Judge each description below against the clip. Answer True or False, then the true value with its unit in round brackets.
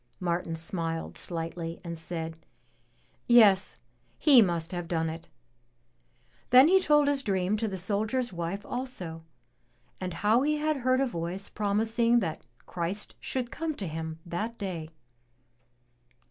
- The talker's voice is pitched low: False (195 Hz)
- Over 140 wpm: False (135 wpm)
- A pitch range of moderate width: False (6.2 semitones)